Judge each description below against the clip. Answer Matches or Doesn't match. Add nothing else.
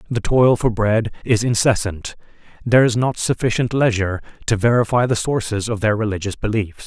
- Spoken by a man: Matches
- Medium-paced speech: Matches